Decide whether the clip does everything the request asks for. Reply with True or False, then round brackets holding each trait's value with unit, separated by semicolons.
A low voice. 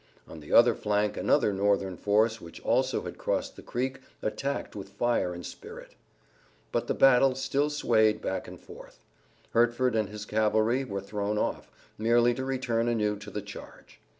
True (110 Hz)